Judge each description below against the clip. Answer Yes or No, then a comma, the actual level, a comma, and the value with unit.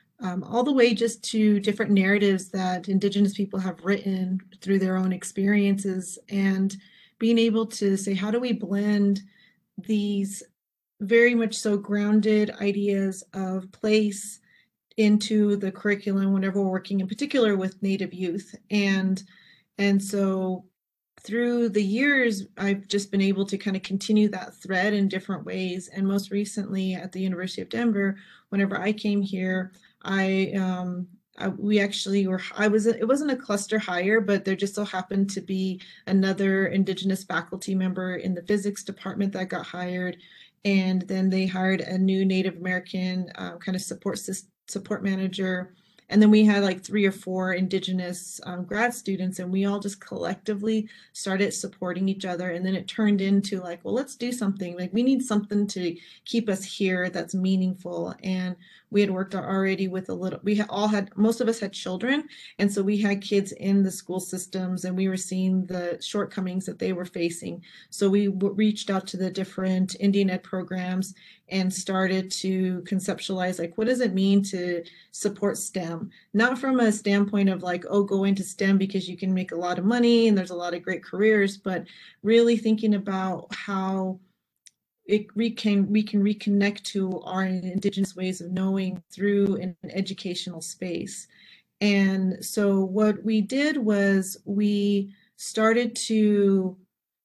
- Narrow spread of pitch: Yes, narrow, 1.7 semitones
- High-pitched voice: Yes, high, 195 Hz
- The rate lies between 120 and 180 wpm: Yes, average, 170 wpm